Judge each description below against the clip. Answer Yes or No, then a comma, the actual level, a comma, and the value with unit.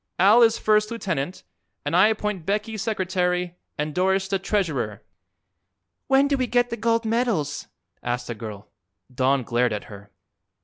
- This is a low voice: No, high, 190 Hz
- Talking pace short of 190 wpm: Yes, average, 150 wpm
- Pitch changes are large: Yes, wide, 8.0 semitones